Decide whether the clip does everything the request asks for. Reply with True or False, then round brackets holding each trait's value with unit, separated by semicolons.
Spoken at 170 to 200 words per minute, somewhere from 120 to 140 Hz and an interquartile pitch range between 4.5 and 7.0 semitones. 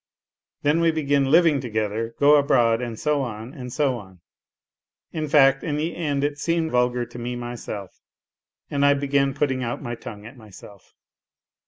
False (175 wpm; 135 Hz; 3.7 semitones)